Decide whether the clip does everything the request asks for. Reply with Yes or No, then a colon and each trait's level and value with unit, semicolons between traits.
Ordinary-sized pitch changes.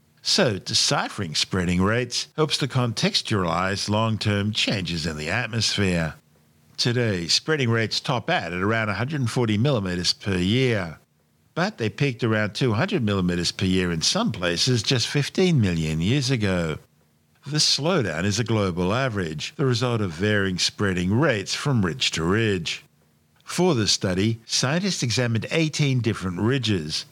No: wide, 5.9 semitones